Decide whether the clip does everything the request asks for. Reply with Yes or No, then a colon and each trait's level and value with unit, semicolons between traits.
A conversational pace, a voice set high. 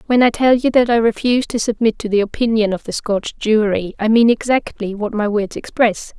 No: fast, 225 wpm; high, 220 Hz